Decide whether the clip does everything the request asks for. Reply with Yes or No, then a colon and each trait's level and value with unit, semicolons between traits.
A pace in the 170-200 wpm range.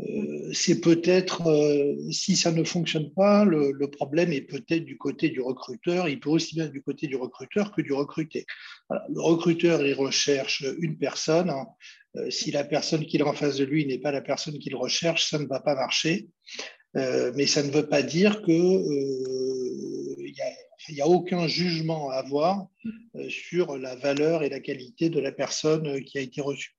Yes: average, 195 wpm